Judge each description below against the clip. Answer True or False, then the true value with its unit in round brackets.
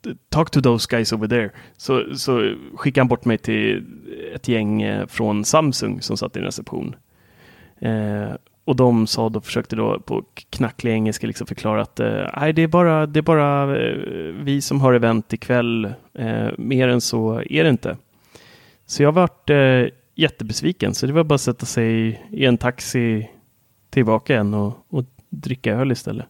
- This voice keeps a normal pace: True (175 wpm)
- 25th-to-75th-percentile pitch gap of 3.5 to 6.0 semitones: True (3.8 semitones)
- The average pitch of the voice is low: True (120 Hz)